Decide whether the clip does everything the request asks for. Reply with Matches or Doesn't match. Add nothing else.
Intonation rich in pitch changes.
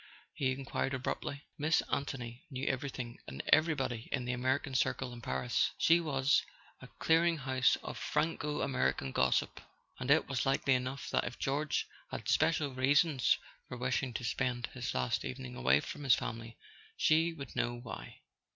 Doesn't match